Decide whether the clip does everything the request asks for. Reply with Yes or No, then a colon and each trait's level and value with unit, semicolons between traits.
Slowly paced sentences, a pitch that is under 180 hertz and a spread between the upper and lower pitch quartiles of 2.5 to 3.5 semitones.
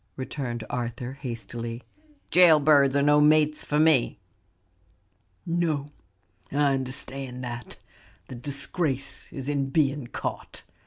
Yes: slow, 110 wpm; medium, 140 Hz; average, 2.9 semitones